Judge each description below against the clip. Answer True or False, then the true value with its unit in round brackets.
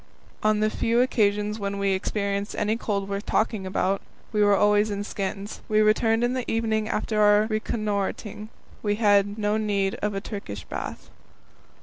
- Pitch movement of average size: False (1.3 semitones)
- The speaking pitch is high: True (210 Hz)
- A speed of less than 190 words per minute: True (175 wpm)